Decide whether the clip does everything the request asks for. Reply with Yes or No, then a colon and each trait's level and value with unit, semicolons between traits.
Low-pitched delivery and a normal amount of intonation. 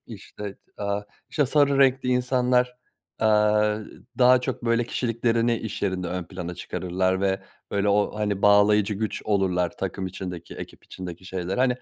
Yes: low, 105 Hz; average, 4.3 semitones